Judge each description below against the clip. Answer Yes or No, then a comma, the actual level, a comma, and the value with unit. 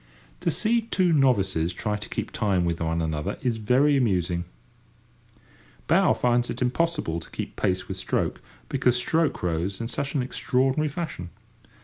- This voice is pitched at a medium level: No, low, 120 Hz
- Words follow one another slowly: No, average, 155 wpm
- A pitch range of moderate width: No, wide, 7.6 semitones